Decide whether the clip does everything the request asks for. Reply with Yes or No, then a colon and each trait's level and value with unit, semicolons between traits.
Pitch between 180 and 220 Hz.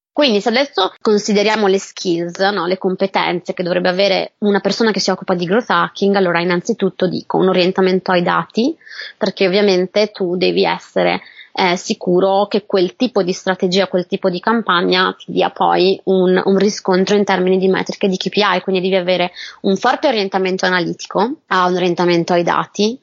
Yes: high, 190 Hz